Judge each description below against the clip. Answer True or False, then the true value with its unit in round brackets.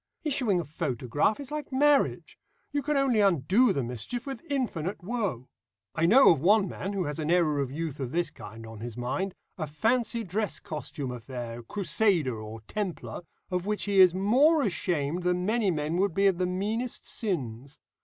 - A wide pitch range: True (7.5 semitones)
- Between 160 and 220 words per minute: True (185 wpm)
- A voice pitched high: False (180 Hz)